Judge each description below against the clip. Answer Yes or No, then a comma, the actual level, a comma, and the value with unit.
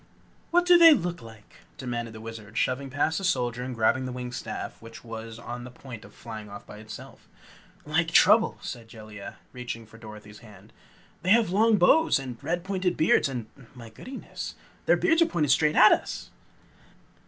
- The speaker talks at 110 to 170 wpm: No, average, 185 wpm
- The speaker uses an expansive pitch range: Yes, wide, 7.5 semitones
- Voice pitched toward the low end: Yes, low, 125 Hz